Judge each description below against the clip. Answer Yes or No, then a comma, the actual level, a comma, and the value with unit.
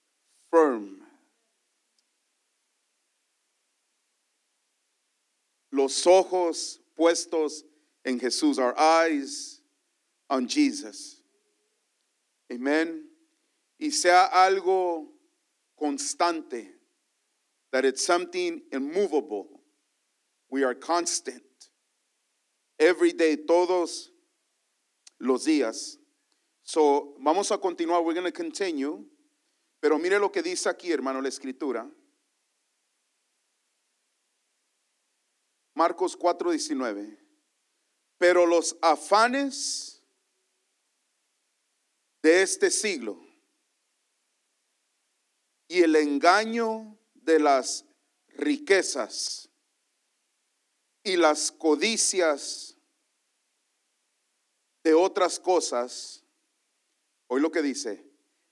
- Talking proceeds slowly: Yes, slow, 70 wpm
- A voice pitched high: Yes, high, 200 Hz